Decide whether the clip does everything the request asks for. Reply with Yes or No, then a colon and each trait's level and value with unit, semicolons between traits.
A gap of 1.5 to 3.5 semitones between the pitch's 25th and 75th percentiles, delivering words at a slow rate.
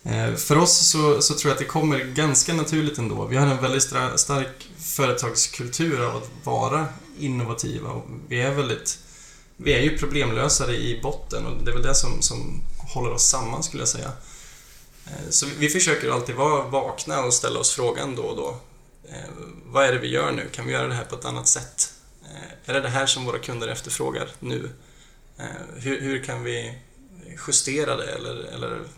No: average, 3.2 semitones; average, 190 wpm